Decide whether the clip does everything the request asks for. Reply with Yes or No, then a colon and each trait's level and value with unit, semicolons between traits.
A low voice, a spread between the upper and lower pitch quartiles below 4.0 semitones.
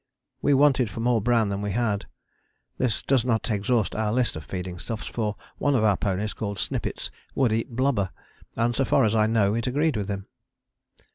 Yes: low, 110 Hz; average, 3.3 semitones